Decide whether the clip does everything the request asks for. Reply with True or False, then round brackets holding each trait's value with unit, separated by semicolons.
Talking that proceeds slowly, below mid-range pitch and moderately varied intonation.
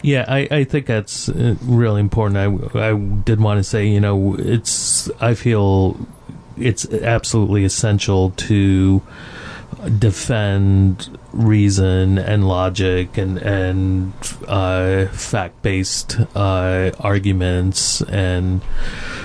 True (105 wpm; 100 Hz; 3.2 semitones)